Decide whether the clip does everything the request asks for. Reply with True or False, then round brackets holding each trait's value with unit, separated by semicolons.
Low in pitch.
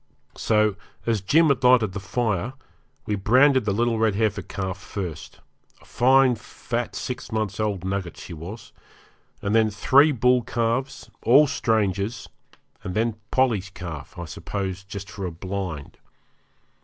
True (105 Hz)